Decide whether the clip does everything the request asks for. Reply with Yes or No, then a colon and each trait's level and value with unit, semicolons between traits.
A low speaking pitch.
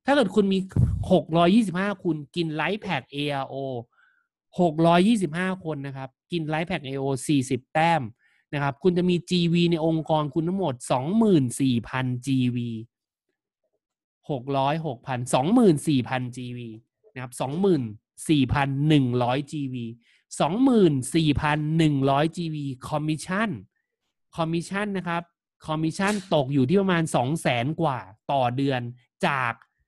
No: medium, 155 Hz